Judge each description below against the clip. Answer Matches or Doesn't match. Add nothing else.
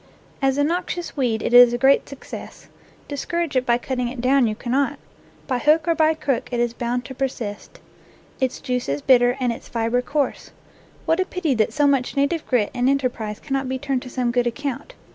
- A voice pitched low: Doesn't match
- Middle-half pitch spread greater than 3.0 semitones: Doesn't match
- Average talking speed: Doesn't match